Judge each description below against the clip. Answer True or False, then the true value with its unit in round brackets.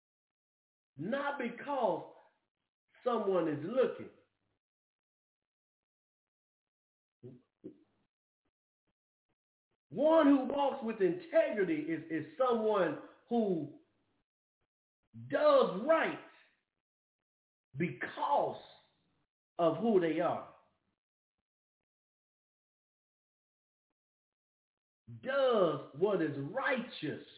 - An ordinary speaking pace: False (55 wpm)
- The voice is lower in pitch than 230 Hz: False (240 Hz)